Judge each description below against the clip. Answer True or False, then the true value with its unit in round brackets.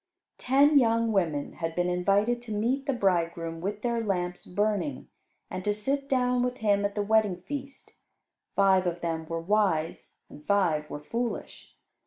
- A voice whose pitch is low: False (205 Hz)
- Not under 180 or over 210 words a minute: False (165 wpm)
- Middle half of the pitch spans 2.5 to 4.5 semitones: False (5.1 semitones)